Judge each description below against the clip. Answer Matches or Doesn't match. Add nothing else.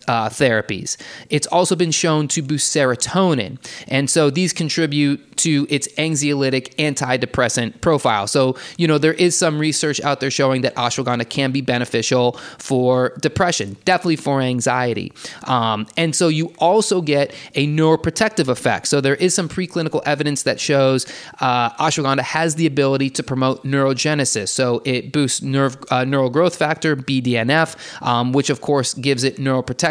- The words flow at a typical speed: Matches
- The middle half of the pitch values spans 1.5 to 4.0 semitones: Matches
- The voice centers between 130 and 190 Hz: Matches